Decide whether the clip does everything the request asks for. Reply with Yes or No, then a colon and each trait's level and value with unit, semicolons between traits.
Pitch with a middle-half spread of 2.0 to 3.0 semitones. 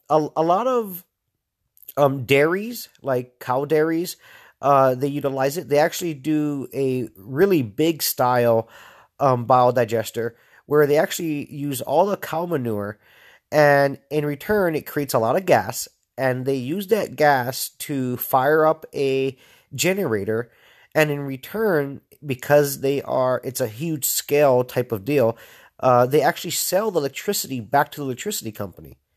No: average, 3.6 semitones